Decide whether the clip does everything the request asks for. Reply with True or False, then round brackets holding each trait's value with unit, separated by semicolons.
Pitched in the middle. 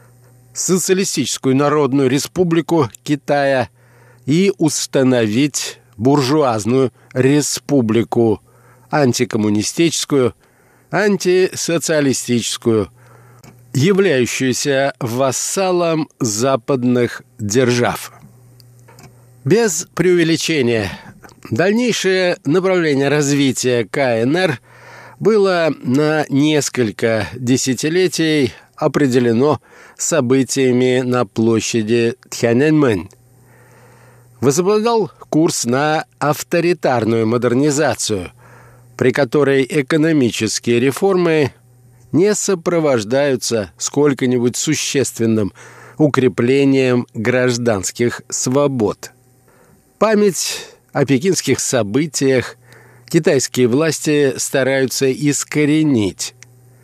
False (130 Hz)